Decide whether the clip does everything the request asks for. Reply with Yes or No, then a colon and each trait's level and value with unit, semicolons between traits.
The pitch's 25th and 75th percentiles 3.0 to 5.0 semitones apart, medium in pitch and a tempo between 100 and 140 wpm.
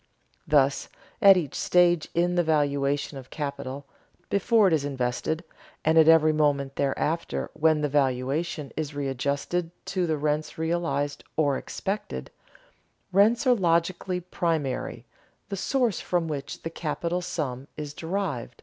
Yes: average, 3.7 semitones; medium, 155 Hz; slow, 135 wpm